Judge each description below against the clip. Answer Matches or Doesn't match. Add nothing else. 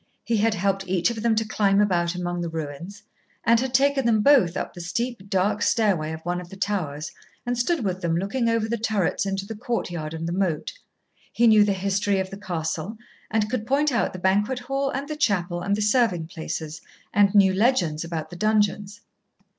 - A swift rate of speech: Matches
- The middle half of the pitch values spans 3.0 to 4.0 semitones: Doesn't match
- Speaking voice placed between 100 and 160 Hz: Doesn't match